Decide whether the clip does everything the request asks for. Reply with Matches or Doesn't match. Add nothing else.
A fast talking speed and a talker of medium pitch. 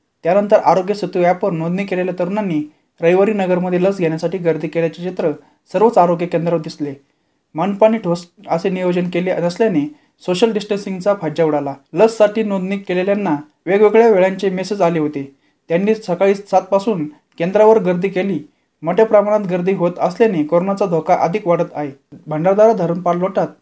Matches